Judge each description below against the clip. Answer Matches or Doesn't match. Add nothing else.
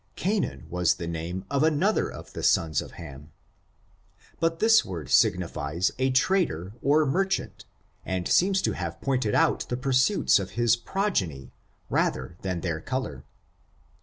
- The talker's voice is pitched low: Matches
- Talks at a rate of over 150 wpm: Doesn't match